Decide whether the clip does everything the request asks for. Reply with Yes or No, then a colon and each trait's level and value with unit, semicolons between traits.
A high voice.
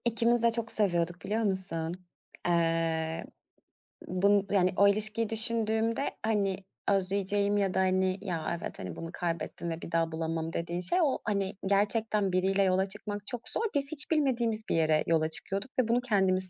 Yes: high, 195 Hz